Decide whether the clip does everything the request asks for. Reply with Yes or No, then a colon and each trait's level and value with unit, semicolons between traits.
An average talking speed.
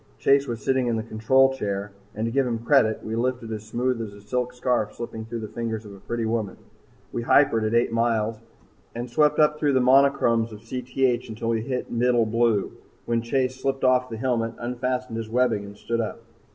No: fast, 210 wpm